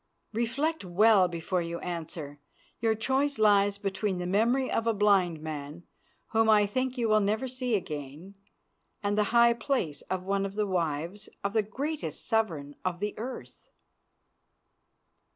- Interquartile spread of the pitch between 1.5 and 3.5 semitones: No, average, 4.4 semitones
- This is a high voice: Yes, high, 205 Hz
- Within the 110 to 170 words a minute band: Yes, average, 150 wpm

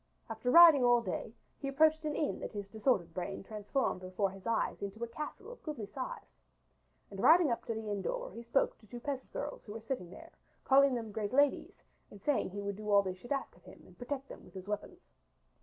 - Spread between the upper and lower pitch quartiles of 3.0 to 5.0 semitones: No, wide, 5.4 semitones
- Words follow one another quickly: Yes, fast, 240 wpm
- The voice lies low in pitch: No, high, 230 Hz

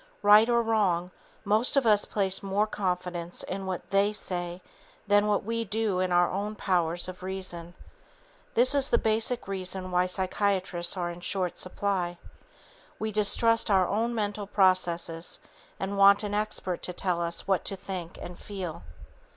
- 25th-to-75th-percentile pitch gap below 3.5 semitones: Yes, average, 2.7 semitones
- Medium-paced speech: Yes, average, 160 wpm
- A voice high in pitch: Yes, high, 195 Hz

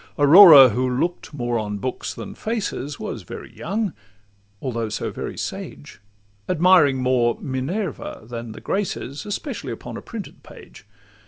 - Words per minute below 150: Yes, average, 140 wpm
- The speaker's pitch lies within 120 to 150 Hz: Yes, low, 135 Hz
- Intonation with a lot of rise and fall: Yes, wide, 7.3 semitones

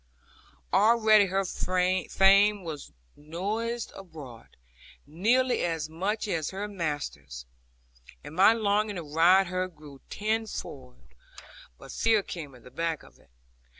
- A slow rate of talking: Yes, slow, 120 wpm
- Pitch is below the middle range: No, medium, 185 Hz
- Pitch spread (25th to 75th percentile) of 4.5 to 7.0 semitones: Yes, average, 5.1 semitones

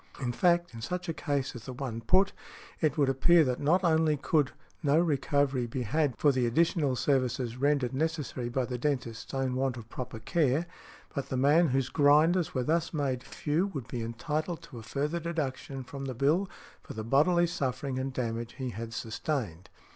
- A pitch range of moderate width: Yes, average, 4.0 semitones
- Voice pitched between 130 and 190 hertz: Yes, low, 135 Hz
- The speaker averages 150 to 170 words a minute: No, average, 190 wpm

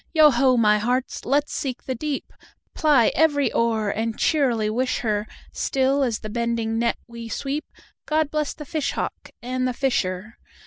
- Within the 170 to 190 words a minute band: No, average, 160 wpm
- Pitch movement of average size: Yes, average, 3.8 semitones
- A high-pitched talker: Yes, very high, 250 Hz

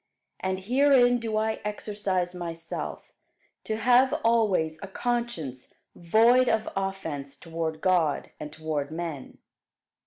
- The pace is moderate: No, slow, 115 wpm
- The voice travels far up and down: Yes, wide, 5.9 semitones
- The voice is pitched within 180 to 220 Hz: Yes, high, 190 Hz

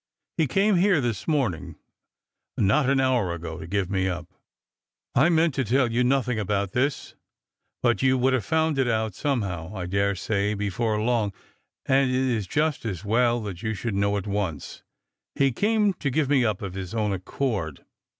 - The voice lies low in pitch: Yes, low, 115 Hz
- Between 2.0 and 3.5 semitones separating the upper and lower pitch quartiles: No, average, 5.2 semitones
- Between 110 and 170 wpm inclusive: No, average, 180 wpm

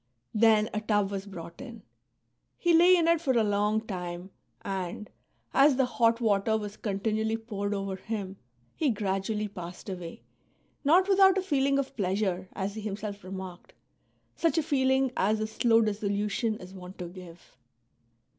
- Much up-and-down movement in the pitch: No, average, 3.8 semitones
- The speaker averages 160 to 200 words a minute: Yes, average, 165 wpm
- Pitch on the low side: No, high, 210 Hz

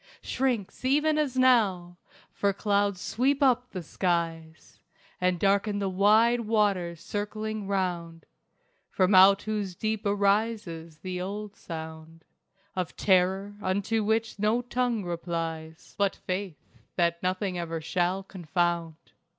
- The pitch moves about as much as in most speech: Yes, average, 3.7 semitones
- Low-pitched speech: No, high, 195 Hz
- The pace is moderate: No, slow, 120 wpm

